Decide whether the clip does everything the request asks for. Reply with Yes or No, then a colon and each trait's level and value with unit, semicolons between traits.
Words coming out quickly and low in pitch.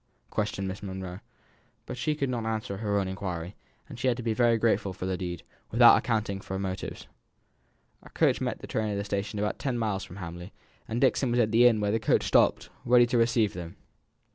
Yes: fast, 220 wpm; low, 105 Hz